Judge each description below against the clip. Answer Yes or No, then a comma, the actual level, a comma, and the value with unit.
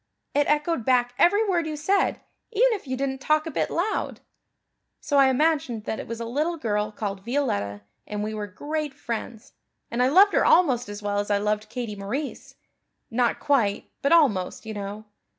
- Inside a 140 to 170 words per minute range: No, average, 190 wpm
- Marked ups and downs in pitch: Yes, wide, 6.3 semitones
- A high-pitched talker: Yes, very high, 250 Hz